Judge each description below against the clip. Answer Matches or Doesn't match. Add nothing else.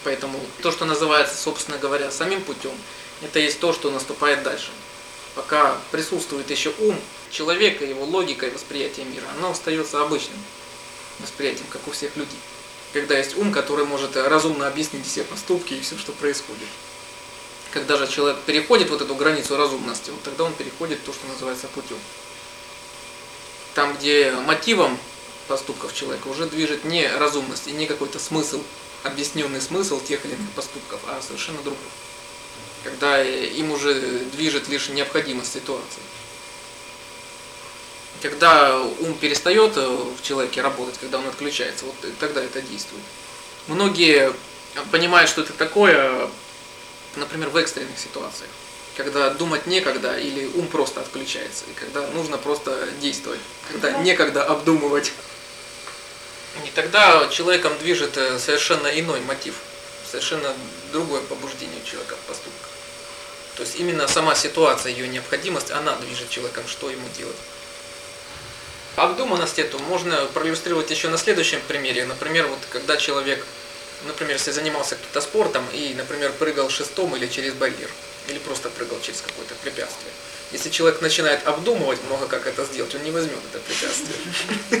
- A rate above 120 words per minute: Matches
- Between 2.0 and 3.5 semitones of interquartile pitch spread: Matches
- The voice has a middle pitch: Matches